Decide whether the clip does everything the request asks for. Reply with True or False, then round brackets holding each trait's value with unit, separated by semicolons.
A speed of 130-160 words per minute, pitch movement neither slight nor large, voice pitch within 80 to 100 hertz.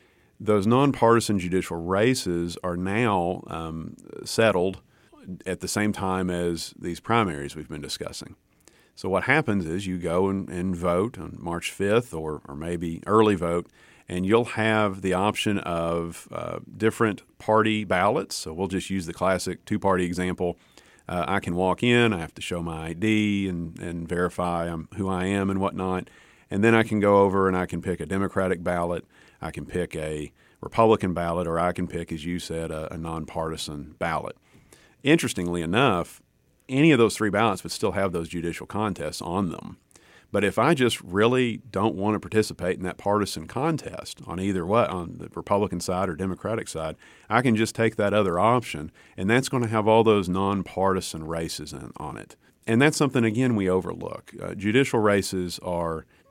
False (180 wpm; 3.7 semitones; 95 Hz)